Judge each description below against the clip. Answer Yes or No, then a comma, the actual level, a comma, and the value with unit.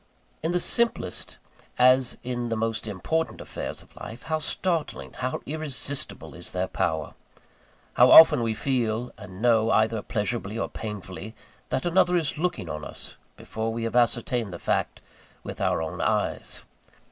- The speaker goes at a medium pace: Yes, average, 155 wpm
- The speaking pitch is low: Yes, low, 120 Hz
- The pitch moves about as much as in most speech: Yes, average, 4.6 semitones